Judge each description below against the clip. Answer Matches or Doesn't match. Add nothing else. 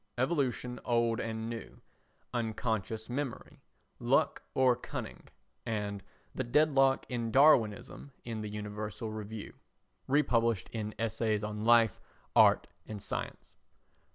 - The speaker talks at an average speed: Doesn't match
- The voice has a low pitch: Matches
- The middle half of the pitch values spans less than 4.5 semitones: Matches